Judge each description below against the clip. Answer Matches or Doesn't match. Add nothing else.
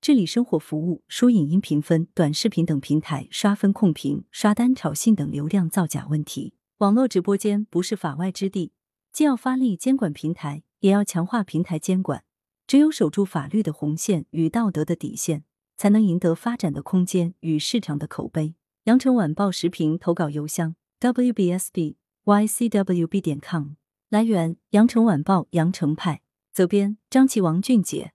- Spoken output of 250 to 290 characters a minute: Matches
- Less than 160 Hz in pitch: Doesn't match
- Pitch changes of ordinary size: Matches